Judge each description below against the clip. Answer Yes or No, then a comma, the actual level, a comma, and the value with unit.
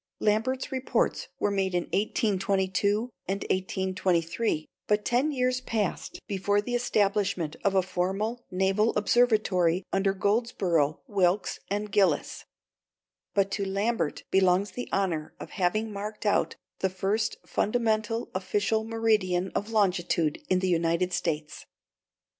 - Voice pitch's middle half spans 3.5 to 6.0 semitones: No, average, 2.9 semitones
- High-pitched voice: Yes, high, 200 Hz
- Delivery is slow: Yes, slow, 125 wpm